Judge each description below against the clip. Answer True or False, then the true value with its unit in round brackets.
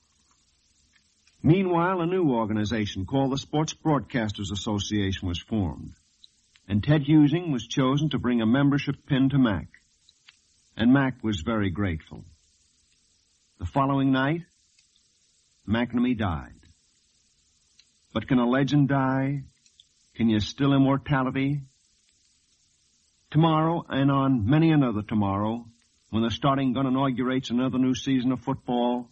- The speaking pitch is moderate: False (120 Hz)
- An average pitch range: False (6.5 semitones)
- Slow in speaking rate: True (120 wpm)